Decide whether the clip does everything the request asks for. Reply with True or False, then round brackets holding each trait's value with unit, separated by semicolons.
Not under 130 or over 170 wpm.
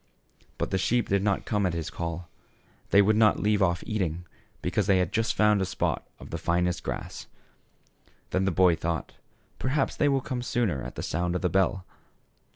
False (195 wpm)